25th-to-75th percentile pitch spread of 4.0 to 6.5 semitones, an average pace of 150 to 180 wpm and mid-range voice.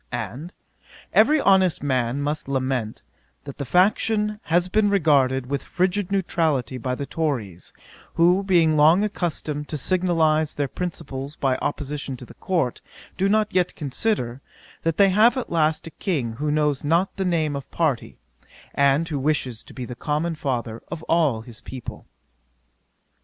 Yes: average, 5.1 semitones; average, 160 wpm; medium, 155 Hz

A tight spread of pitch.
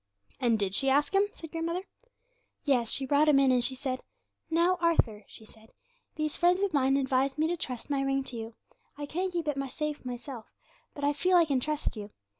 No: average, 4.2 semitones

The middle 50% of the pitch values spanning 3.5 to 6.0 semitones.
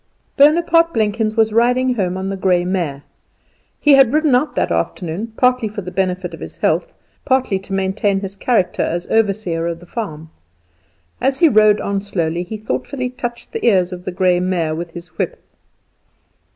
Yes: average, 5.2 semitones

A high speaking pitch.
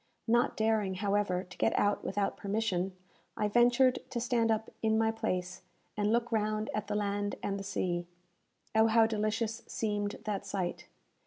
Yes: high, 210 Hz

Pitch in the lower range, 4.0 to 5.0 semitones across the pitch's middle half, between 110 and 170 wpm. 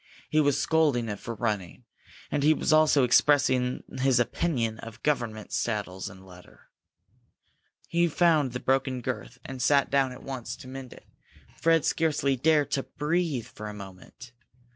Yes: low, 130 Hz; average, 4.3 semitones; average, 160 wpm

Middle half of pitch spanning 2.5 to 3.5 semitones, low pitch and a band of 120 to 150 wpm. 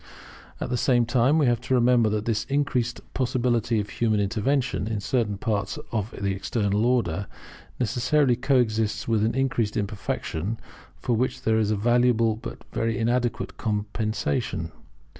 Yes: average, 2.9 semitones; low, 115 Hz; average, 145 wpm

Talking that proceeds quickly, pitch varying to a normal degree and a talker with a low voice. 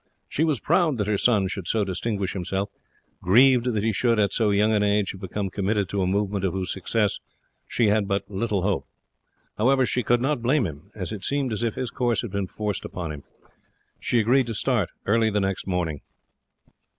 Yes: fast, 210 wpm; average, 3.4 semitones; low, 105 Hz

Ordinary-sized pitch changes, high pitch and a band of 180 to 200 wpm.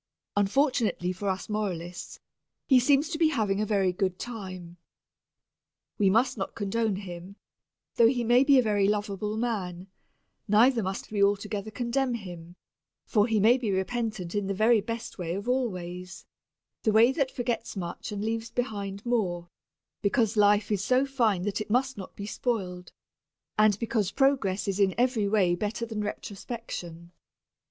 No: average, 3.6 semitones; high, 210 Hz; average, 160 wpm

